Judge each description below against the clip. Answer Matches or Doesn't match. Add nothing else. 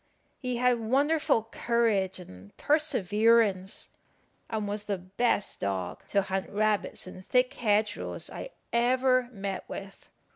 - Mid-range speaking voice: Doesn't match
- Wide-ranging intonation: Doesn't match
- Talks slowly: Matches